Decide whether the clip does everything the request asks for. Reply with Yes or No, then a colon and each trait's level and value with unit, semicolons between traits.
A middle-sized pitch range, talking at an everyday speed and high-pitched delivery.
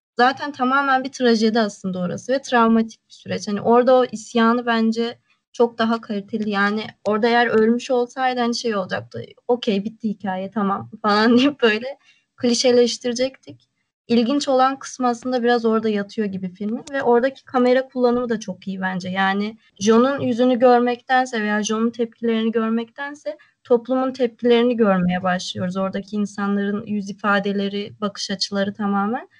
No: average, 3.3 semitones; fast, 145 wpm; high, 230 Hz